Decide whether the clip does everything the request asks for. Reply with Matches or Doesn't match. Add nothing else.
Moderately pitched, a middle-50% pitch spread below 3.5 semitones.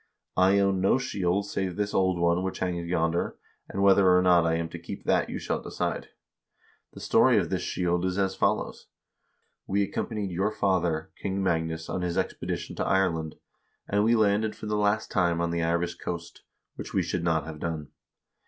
Doesn't match